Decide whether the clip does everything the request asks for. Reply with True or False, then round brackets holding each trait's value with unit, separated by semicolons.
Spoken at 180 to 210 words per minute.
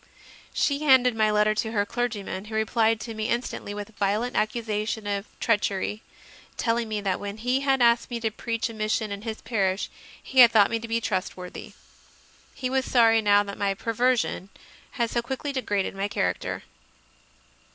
True (185 wpm)